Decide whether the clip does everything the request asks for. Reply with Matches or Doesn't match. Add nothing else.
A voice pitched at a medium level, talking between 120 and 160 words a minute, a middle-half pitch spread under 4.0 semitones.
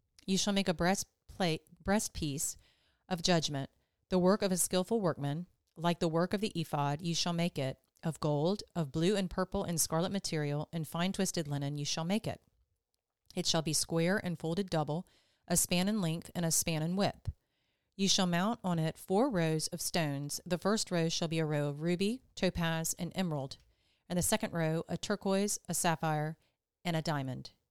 Doesn't match